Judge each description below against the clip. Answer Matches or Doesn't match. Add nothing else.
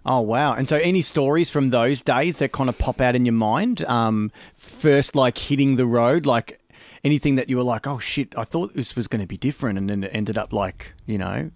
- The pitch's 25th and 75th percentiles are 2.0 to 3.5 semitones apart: Doesn't match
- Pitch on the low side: Matches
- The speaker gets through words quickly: Matches